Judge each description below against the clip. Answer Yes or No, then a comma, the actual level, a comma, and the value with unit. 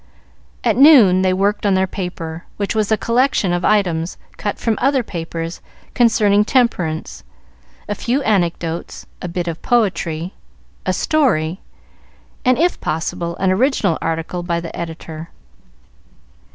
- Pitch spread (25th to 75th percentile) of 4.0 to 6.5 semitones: Yes, average, 4.6 semitones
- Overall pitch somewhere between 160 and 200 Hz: Yes, medium, 185 Hz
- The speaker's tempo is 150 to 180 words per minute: No, slow, 135 wpm